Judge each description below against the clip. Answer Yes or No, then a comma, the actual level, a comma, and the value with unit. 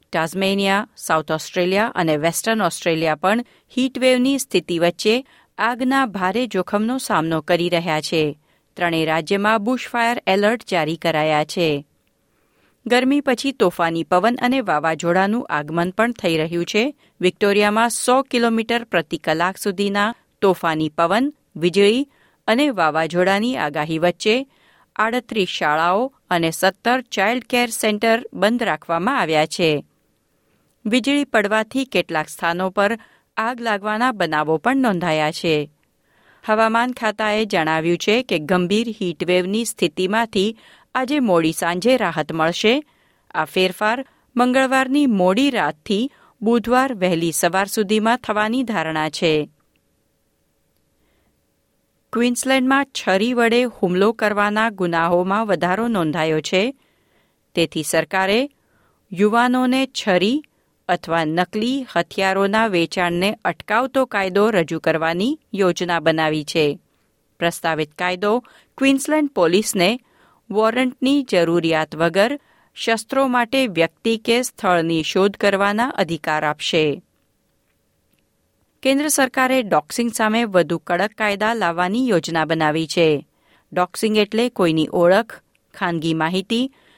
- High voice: Yes, high, 200 Hz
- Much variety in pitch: Yes, wide, 5.8 semitones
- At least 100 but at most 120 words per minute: Yes, average, 105 wpm